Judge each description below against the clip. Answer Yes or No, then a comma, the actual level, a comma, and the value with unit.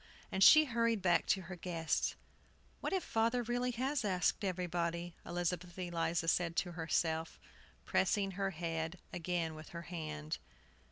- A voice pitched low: No, medium, 175 Hz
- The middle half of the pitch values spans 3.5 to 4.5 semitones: No, average, 3.0 semitones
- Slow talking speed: No, average, 145 wpm